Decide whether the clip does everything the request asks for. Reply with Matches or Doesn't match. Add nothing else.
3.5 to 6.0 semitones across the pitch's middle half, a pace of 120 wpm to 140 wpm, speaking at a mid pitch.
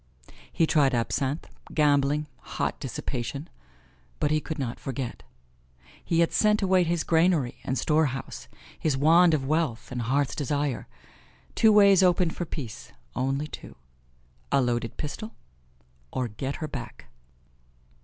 Matches